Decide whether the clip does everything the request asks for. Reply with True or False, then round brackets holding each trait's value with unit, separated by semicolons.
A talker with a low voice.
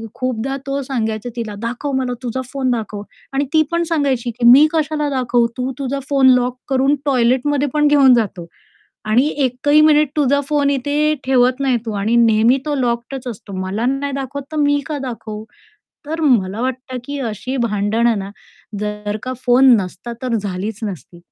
False (255 Hz)